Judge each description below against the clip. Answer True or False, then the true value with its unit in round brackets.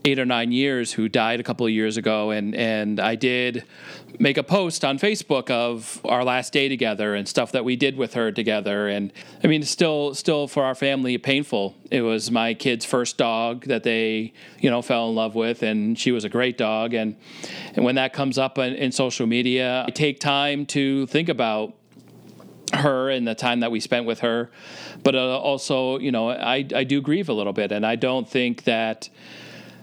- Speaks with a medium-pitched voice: False (125 Hz)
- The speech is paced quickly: True (215 wpm)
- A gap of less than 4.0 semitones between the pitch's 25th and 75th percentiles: True (3.3 semitones)